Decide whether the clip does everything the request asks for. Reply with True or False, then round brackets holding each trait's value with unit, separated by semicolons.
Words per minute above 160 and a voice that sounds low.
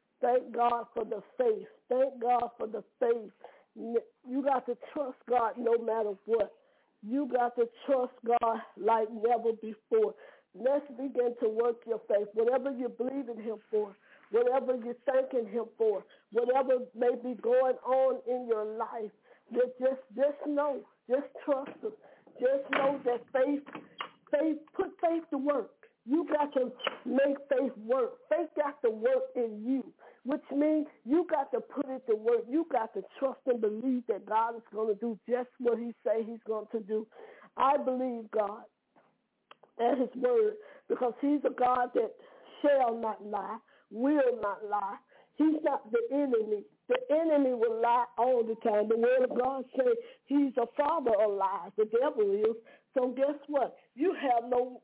False (170 wpm; 255 Hz)